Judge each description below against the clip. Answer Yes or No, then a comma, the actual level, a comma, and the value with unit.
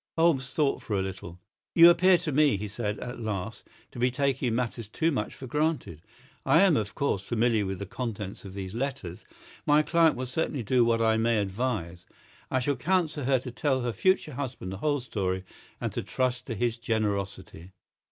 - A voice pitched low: Yes, low, 120 Hz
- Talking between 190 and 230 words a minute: Yes, average, 195 wpm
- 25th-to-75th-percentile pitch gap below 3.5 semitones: No, wide, 5.6 semitones